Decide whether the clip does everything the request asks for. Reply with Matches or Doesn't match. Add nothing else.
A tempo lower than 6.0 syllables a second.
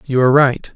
Doesn't match